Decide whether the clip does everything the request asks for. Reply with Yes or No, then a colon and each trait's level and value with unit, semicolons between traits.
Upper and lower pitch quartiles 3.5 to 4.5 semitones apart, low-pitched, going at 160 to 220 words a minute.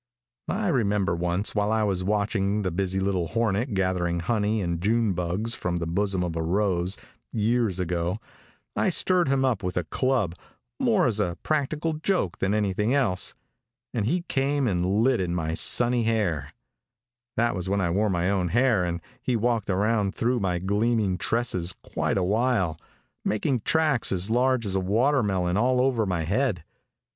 No: average, 4.9 semitones; low, 105 Hz; average, 170 wpm